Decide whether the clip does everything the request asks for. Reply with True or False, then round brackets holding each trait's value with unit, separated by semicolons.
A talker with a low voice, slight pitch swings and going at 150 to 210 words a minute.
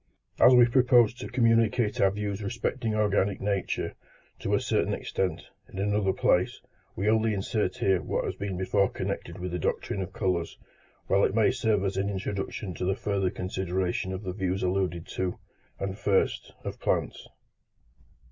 True (100 Hz; 2.3 semitones; 165 wpm)